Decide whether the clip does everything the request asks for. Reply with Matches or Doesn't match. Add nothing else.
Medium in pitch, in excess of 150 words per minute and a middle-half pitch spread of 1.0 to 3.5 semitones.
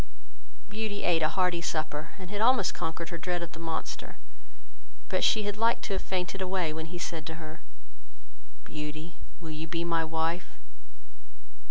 Matches